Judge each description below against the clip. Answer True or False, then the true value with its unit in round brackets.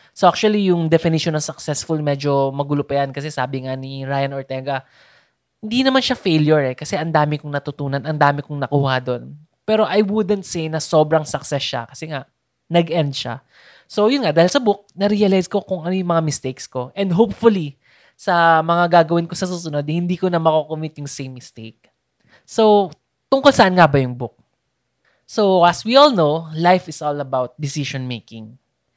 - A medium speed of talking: False (190 wpm)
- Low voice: False (155 Hz)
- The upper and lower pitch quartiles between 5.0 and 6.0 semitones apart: False (4.4 semitones)